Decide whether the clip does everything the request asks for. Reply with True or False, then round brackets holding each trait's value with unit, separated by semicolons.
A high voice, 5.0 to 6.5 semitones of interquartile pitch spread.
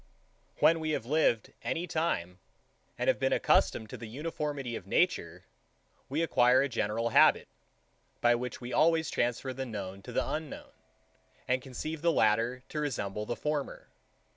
False (125 Hz; 5.3 semitones)